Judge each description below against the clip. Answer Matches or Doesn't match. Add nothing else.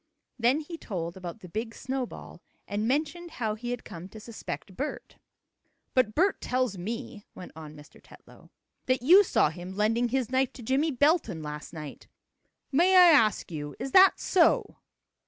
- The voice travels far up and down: Matches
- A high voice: Matches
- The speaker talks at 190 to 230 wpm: Doesn't match